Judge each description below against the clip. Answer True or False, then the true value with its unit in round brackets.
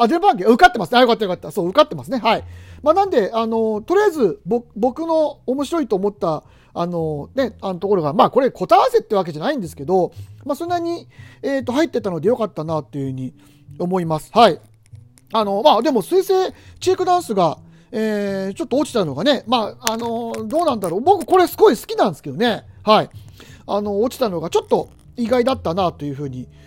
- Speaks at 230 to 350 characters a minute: False (400 characters per minute)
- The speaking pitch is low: False (225 Hz)